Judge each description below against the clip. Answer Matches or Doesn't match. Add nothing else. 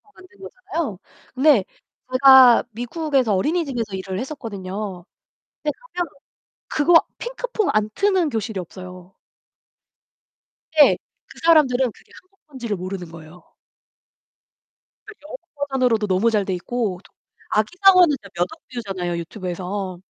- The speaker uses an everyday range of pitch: Doesn't match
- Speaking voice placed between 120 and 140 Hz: Doesn't match